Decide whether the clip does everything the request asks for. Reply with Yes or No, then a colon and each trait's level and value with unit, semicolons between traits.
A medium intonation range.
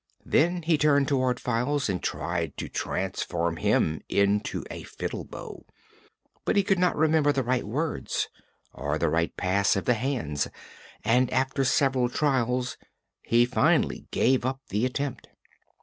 No: wide, 5.8 semitones